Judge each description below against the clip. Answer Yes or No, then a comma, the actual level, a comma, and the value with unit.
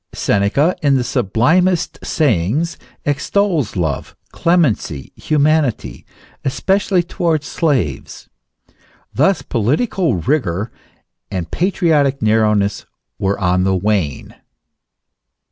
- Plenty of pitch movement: Yes, wide, 8.4 semitones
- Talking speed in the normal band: No, slow, 85 wpm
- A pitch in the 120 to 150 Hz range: Yes, low, 135 Hz